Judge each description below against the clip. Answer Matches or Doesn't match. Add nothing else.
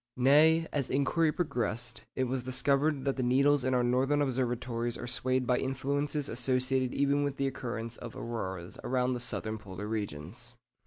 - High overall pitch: Doesn't match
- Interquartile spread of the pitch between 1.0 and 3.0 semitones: Matches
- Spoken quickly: Doesn't match